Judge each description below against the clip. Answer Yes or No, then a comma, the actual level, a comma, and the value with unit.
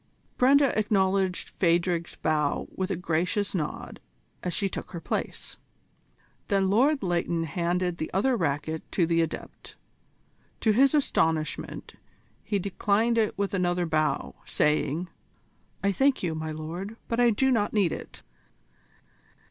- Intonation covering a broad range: No, average, 4.1 semitones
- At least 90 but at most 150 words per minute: Yes, slow, 135 wpm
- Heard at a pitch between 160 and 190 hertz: Yes, medium, 185 Hz